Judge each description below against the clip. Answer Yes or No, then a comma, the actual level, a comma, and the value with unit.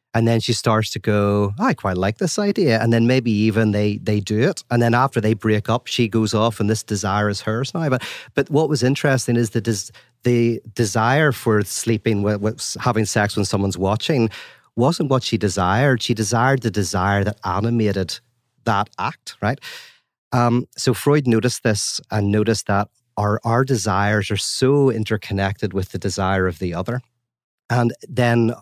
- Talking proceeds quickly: No, average, 185 wpm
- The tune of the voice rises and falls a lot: No, average, 2.8 semitones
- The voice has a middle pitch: No, low, 115 Hz